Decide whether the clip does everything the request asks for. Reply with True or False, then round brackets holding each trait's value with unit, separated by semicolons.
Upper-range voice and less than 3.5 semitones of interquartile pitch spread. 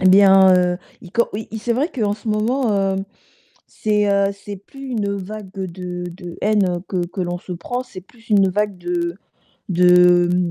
True (195 Hz; 2.9 semitones)